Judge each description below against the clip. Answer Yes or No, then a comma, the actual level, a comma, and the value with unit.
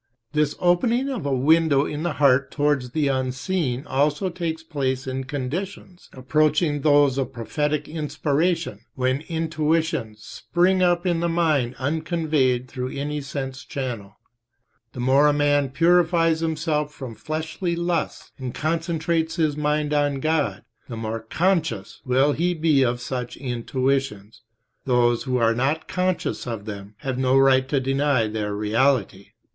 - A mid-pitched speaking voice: Yes, medium, 145 Hz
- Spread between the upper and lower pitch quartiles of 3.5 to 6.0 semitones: Yes, average, 3.9 semitones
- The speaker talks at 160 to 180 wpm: No, average, 145 wpm